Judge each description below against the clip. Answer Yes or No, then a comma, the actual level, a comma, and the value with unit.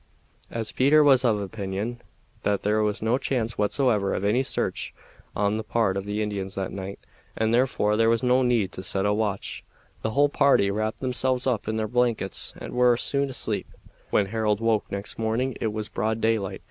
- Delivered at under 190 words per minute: No, average, 195 wpm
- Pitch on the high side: No, low, 110 Hz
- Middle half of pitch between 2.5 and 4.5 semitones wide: Yes, average, 3.1 semitones